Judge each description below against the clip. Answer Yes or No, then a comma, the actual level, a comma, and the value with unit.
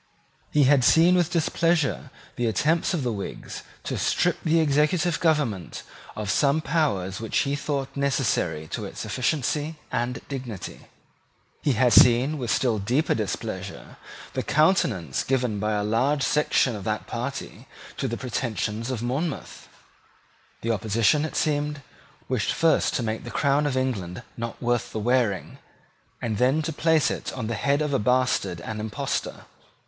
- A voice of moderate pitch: No, low, 130 Hz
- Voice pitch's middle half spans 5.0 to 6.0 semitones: Yes, average, 5.3 semitones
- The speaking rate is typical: Yes, average, 155 wpm